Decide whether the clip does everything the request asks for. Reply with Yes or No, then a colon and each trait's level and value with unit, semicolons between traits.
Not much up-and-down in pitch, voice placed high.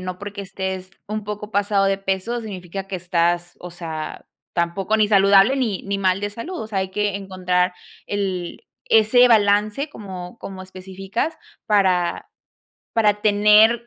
Yes: narrow, 2.2 semitones; high, 195 Hz